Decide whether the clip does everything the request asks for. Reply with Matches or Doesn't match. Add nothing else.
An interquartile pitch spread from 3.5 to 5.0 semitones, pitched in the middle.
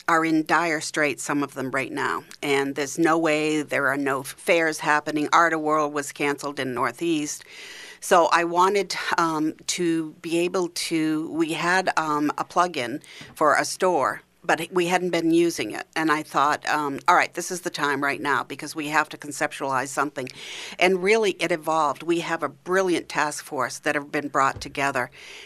Doesn't match